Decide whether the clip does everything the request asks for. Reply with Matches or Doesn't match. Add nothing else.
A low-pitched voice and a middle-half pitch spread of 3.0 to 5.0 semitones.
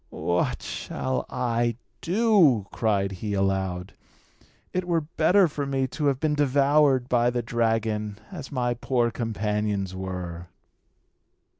Doesn't match